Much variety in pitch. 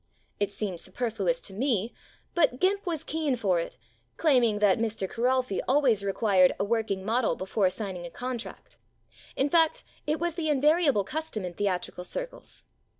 Yes: wide, 7.0 semitones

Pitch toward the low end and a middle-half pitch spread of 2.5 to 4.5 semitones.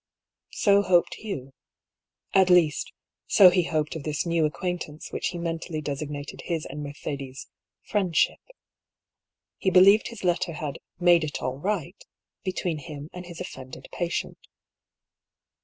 No: medium, 170 Hz; average, 3.5 semitones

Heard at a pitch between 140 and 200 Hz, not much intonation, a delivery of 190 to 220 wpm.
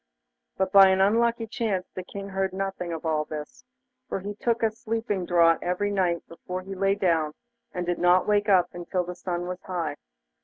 Yes: medium, 185 Hz; narrow, 2.3 semitones; average, 195 wpm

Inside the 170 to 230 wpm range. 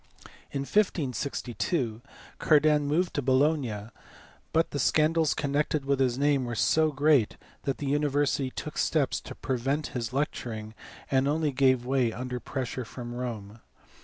No: average, 140 wpm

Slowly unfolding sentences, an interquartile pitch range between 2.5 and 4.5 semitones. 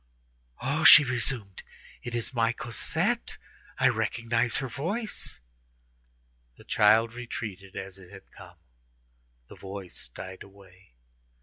Yes: slow, 115 wpm; average, 4.0 semitones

